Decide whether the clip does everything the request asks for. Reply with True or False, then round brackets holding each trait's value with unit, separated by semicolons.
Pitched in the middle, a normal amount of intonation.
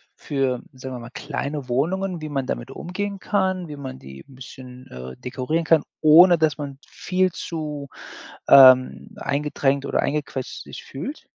True (145 Hz; 4.3 semitones)